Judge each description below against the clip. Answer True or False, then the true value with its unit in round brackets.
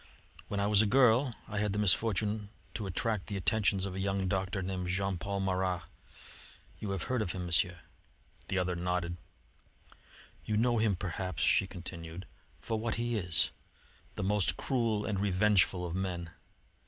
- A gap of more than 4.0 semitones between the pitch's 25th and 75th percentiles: False (2.8 semitones)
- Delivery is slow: False (165 wpm)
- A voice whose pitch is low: True (95 Hz)